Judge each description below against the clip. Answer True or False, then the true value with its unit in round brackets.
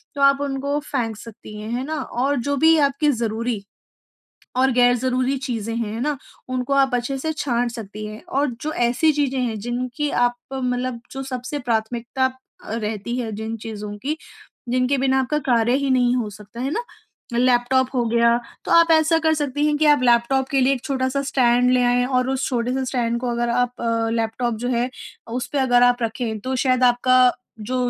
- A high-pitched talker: True (250 Hz)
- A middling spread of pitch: False (2.3 semitones)